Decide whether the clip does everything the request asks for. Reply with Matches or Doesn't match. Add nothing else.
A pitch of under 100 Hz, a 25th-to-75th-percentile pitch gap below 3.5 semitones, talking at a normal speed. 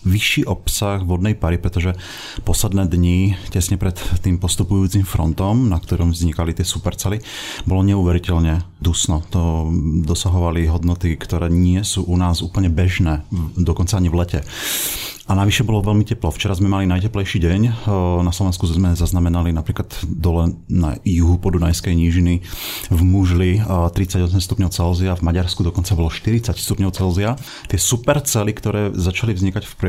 Matches